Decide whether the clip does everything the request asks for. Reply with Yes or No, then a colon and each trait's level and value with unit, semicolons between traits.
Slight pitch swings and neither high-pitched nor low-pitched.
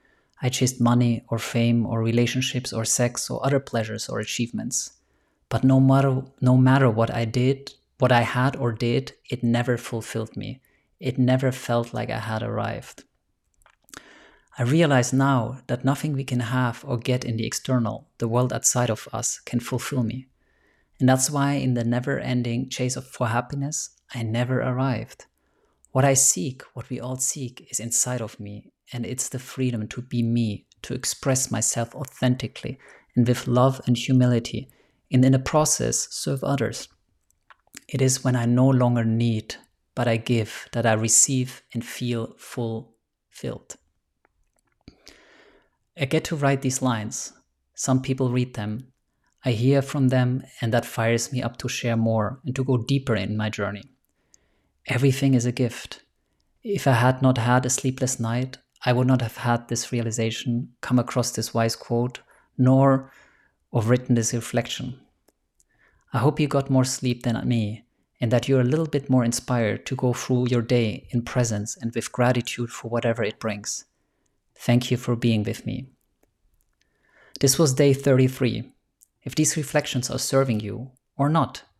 No: narrow, 2.0 semitones; low, 125 Hz